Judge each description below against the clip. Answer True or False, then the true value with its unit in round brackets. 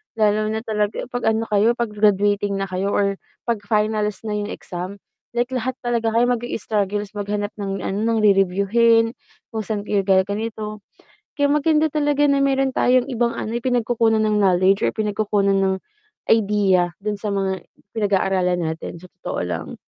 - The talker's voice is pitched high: True (210 Hz)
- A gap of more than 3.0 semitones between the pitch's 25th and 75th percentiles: False (2.6 semitones)